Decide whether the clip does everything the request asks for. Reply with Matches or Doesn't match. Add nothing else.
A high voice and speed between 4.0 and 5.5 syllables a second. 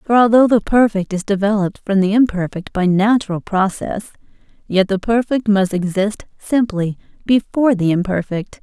Matches